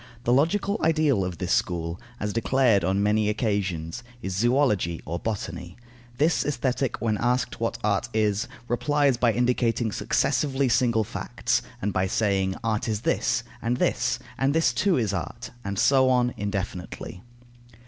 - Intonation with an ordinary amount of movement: Yes, average, 4.5 semitones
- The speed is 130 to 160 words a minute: Yes, average, 150 wpm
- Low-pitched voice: Yes, low, 115 Hz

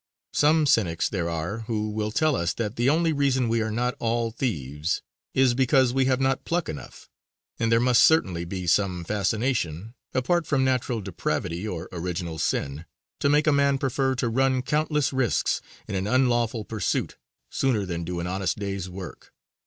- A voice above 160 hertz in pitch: No, low, 115 Hz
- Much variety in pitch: Yes, wide, 6.3 semitones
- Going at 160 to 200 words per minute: Yes, average, 175 wpm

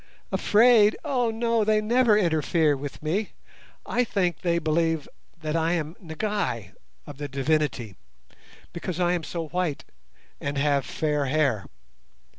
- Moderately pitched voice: Yes, medium, 165 Hz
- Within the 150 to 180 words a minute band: No, slow, 135 wpm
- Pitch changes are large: Yes, wide, 5.9 semitones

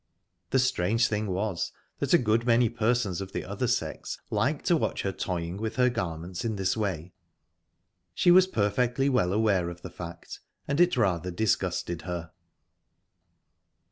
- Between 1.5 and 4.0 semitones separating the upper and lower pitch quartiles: No, average, 4.9 semitones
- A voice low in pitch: Yes, low, 100 Hz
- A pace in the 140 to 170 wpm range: Yes, average, 160 wpm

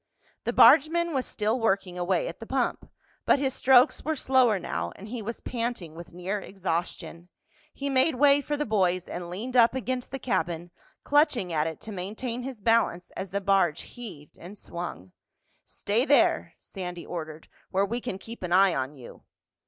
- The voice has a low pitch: No, high, 205 Hz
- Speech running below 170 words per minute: No, average, 180 wpm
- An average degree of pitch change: No, wide, 6.2 semitones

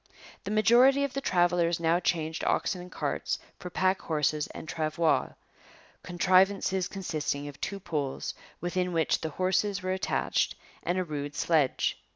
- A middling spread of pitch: Yes, average, 3.1 semitones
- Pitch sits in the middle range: Yes, medium, 175 Hz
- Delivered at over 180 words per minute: No, average, 150 wpm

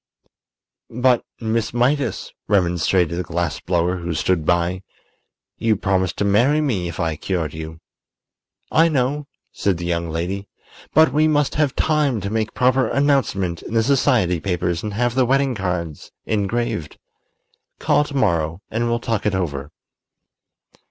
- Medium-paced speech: Yes, average, 150 wpm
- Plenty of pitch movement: Yes, wide, 6.5 semitones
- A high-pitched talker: No, low, 100 Hz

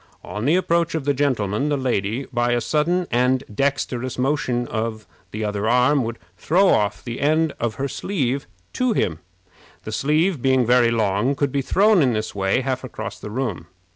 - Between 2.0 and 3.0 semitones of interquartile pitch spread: No, average, 4.3 semitones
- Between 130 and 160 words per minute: No, average, 175 wpm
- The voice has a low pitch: Yes, low, 130 Hz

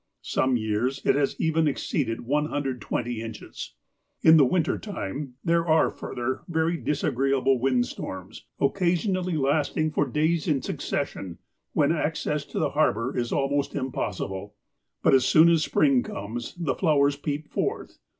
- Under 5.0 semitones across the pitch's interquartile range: Yes, average, 4.3 semitones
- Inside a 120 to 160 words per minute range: Yes, average, 145 wpm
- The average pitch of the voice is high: No, medium, 140 Hz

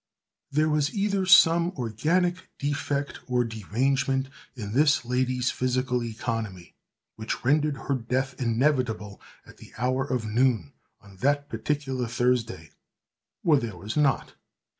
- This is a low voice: Yes, low, 130 Hz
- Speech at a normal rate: No, slow, 125 wpm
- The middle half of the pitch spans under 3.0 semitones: No, average, 3.9 semitones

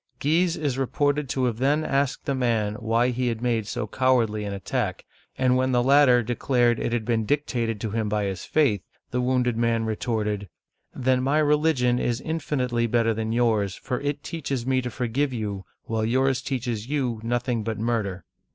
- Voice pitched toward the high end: No, low, 120 Hz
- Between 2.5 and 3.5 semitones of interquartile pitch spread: Yes, average, 3.0 semitones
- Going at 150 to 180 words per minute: No, average, 190 wpm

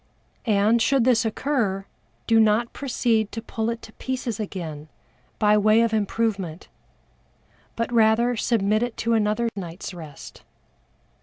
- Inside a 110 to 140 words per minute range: Yes, slow, 135 wpm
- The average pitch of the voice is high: Yes, high, 220 Hz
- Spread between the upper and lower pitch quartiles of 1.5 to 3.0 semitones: Yes, narrow, 2.4 semitones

